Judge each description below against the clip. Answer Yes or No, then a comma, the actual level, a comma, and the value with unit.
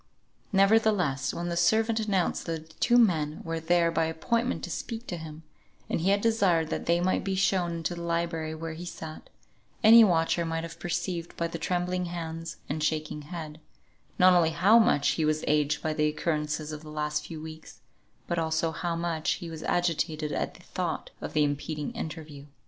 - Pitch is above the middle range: No, medium, 165 Hz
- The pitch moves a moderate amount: No, narrow, 2.2 semitones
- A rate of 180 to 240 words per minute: Yes, average, 190 wpm